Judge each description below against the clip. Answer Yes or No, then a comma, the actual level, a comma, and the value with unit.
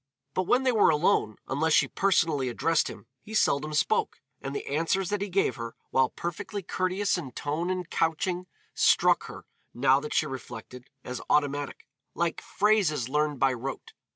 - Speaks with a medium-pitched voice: Yes, medium, 155 Hz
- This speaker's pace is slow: No, average, 170 wpm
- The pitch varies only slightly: No, average, 5.3 semitones